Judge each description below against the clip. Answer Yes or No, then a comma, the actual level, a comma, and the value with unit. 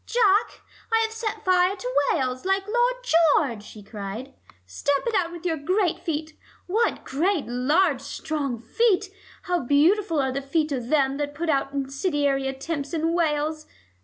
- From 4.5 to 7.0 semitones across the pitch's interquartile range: Yes, wide, 5.4 semitones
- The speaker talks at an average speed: Yes, average, 160 wpm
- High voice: Yes, very high, 310 Hz